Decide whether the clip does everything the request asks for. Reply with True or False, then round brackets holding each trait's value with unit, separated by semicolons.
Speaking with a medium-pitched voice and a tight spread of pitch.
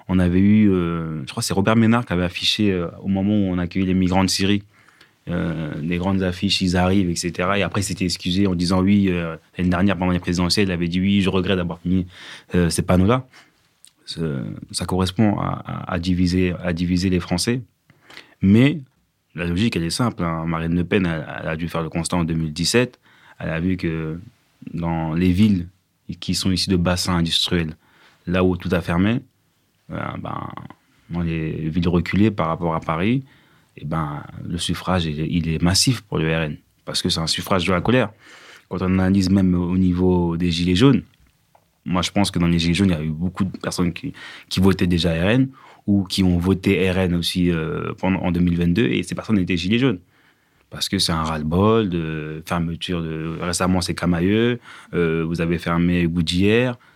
False (90 Hz; 2.1 semitones)